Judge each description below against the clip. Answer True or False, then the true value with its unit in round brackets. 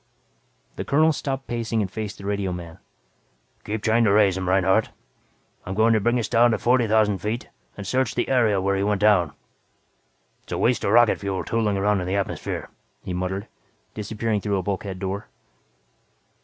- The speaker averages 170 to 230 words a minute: True (180 wpm)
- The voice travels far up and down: False (2.9 semitones)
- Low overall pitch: True (105 Hz)